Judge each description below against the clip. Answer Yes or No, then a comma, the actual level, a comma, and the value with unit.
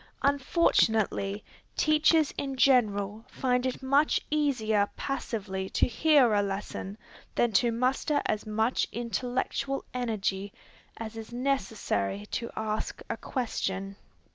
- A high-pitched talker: Yes, high, 230 Hz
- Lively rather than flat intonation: No, average, 4.5 semitones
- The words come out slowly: Yes, slow, 115 wpm